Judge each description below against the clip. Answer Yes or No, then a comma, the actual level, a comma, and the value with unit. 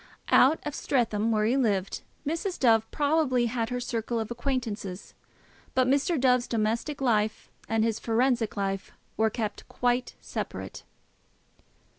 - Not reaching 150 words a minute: Yes, slow, 135 wpm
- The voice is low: No, high, 235 Hz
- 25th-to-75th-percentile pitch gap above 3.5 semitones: No, average, 3.0 semitones